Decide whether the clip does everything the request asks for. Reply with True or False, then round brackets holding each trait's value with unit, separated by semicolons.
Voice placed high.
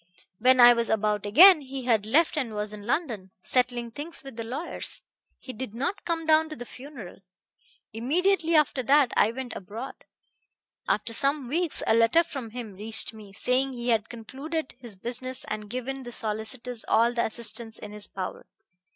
True (245 Hz)